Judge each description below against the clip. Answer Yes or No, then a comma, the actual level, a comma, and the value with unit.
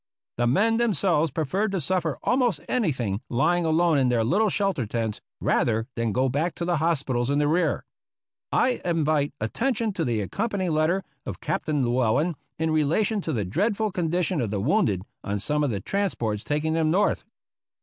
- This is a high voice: No, medium, 155 Hz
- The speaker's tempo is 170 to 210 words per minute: Yes, average, 180 wpm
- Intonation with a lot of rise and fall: Yes, wide, 7.2 semitones